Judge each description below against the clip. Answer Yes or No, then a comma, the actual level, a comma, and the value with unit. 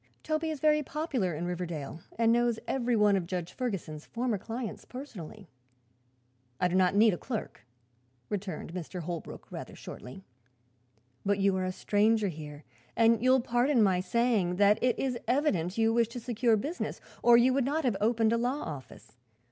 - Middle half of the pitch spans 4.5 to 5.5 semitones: Yes, average, 5.1 semitones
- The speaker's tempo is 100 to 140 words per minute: No, average, 175 wpm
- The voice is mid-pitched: No, high, 220 Hz